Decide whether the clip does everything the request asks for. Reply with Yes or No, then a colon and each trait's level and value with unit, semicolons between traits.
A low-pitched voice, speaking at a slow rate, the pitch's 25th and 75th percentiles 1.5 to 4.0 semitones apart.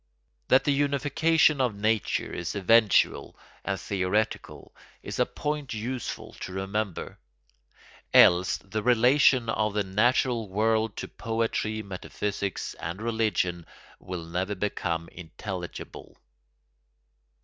Yes: low, 105 Hz; slow, 105 wpm; average, 3.7 semitones